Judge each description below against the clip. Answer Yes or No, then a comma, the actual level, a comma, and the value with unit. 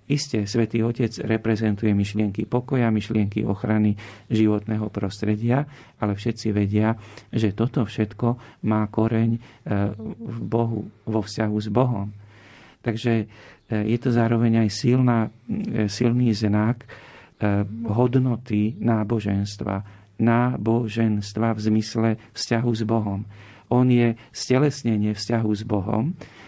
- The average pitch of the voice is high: No, low, 110 Hz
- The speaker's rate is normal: No, slow, 105 wpm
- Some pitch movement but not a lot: No, narrow, 1.7 semitones